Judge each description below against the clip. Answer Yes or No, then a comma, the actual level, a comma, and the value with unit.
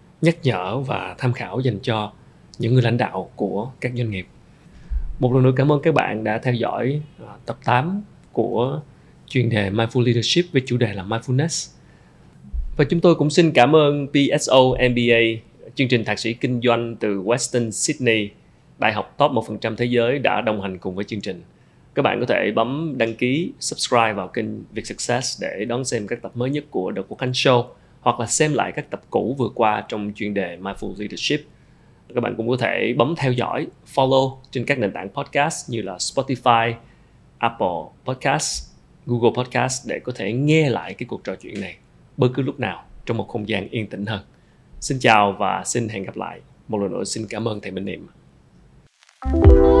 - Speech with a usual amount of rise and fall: Yes, average, 3.5 semitones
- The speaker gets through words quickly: No, average, 200 wpm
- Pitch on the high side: No, low, 120 Hz